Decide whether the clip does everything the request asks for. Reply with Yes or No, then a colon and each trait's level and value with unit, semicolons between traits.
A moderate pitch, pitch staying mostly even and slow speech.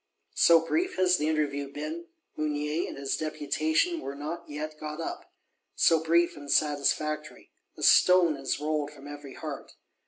No: medium, 155 Hz; narrow, 2.2 semitones; average, 155 wpm